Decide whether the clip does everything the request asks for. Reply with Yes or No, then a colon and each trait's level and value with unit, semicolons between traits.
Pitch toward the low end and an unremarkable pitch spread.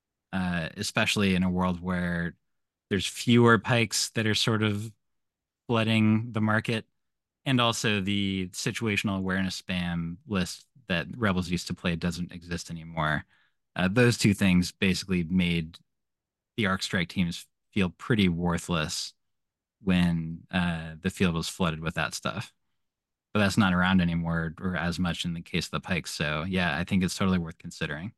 Yes: very low, 90 Hz; average, 3.6 semitones